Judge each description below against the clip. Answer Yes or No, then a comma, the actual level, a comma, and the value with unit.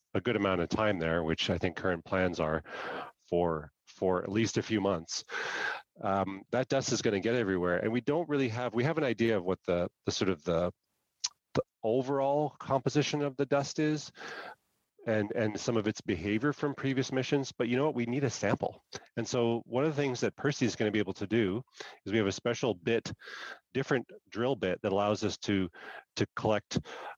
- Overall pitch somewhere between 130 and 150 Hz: No, low, 115 Hz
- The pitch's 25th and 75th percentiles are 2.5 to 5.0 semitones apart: No, wide, 5.6 semitones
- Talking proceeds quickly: Yes, fast, 215 wpm